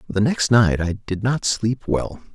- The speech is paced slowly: No, fast, 205 wpm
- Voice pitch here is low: Yes, low, 110 Hz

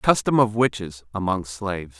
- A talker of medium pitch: No, low, 100 Hz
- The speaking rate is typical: Yes, average, 150 wpm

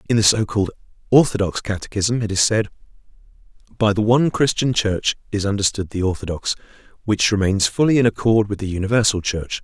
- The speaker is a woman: No, male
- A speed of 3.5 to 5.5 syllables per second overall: No, 6.0 syllables/s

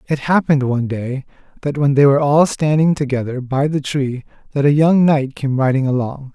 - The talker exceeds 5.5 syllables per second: No, 5.4 syllables/s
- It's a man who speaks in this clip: Yes, male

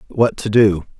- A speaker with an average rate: Yes, average, 180 wpm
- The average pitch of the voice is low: Yes, low, 100 Hz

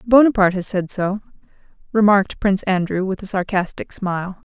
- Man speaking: No, female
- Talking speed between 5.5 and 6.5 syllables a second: Yes, 5.8 syllables/s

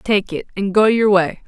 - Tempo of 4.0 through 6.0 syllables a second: Yes, 4.6 syllables/s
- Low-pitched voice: No, high, 200 Hz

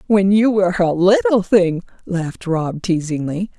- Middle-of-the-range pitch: Yes, medium, 180 Hz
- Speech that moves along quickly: No, average, 150 wpm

